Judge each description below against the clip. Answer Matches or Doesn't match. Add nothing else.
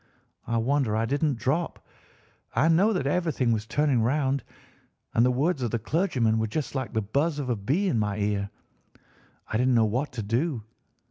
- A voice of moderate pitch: Doesn't match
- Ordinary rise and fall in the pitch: Matches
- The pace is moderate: Matches